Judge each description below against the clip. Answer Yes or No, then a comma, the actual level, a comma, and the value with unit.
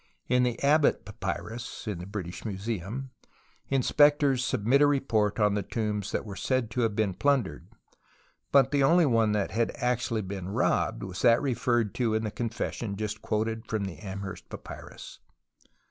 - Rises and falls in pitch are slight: No, average, 3.7 semitones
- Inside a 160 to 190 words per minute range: Yes, average, 165 wpm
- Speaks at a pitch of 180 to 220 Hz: No, low, 115 Hz